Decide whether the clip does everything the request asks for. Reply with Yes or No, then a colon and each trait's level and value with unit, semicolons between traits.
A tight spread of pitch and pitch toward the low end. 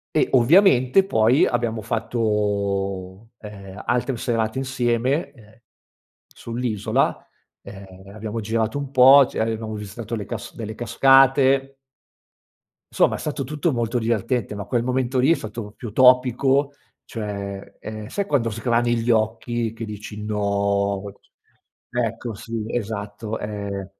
No: average, 3.2 semitones; low, 115 Hz